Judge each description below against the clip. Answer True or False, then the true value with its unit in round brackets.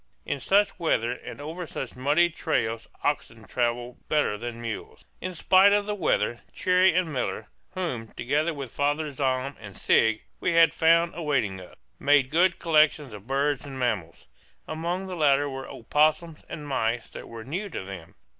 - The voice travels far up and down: True (5.7 semitones)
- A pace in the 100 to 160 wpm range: False (170 wpm)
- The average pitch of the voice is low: False (145 Hz)